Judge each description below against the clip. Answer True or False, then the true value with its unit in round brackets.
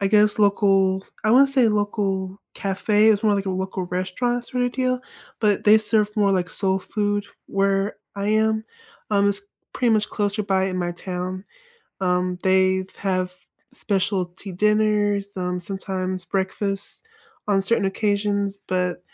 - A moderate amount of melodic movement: False (2.0 semitones)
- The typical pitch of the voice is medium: False (200 Hz)